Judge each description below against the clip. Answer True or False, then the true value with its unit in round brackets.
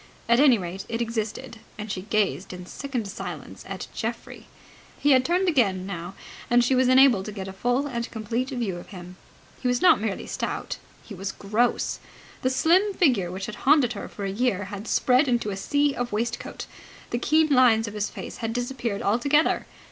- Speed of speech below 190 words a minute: False (195 wpm)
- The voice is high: True (235 Hz)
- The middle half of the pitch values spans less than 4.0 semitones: False (4.5 semitones)